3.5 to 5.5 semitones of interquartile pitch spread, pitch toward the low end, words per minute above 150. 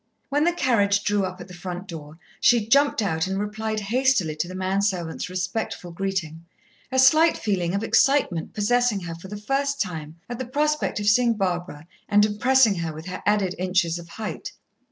No: average, 5.2 semitones; high, 200 Hz; average, 190 wpm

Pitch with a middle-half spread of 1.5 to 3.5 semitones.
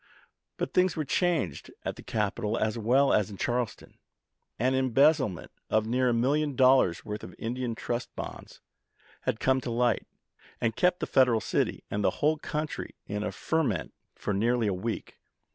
No: average, 3.9 semitones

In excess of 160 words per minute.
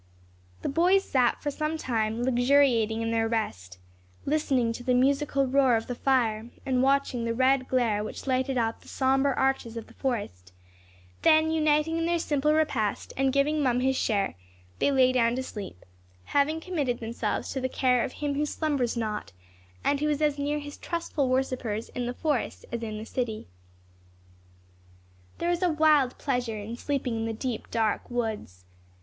Yes: average, 180 wpm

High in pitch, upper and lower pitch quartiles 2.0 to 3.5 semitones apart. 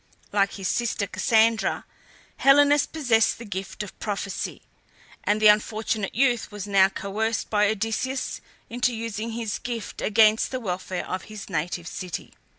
Yes: high, 215 Hz; average, 2.7 semitones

